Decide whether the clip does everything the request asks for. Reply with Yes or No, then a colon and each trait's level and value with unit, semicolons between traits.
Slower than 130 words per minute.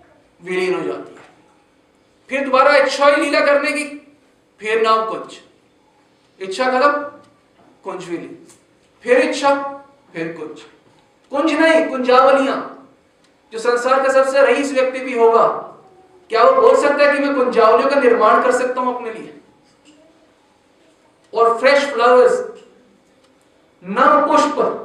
Yes: average, 120 wpm